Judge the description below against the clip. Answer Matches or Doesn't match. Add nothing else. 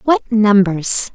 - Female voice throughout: Matches